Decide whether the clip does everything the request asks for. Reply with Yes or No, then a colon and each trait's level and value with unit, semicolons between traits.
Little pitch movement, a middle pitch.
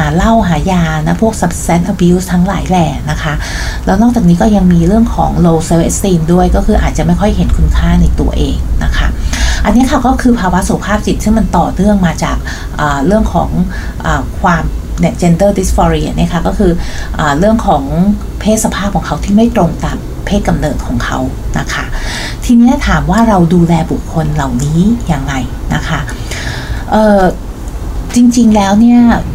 No: average, 4.8 semitones; medium, 180 Hz